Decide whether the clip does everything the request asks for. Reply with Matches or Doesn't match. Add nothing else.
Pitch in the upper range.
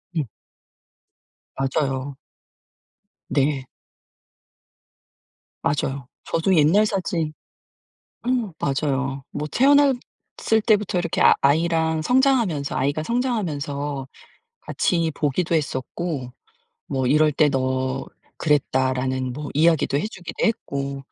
Doesn't match